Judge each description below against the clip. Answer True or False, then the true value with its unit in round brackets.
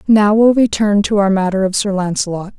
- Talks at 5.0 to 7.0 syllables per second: True (5.4 syllables/s)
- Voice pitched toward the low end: False (200 Hz)